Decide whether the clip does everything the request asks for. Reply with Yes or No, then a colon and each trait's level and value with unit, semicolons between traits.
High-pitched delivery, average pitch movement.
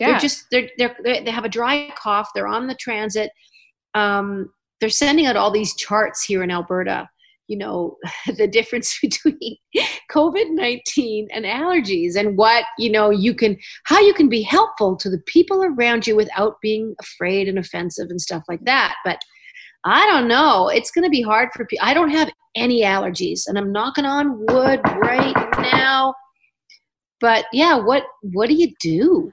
No: high, 235 Hz; wide, 6.4 semitones